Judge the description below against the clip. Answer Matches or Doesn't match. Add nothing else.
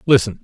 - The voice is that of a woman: Doesn't match